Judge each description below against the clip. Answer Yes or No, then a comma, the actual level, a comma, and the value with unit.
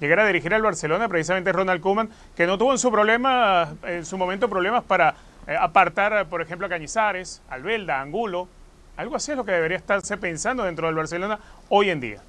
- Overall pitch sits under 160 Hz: No, high, 190 Hz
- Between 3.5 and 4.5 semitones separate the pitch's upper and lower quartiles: Yes, average, 3.8 semitones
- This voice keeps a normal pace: No, fast, 195 wpm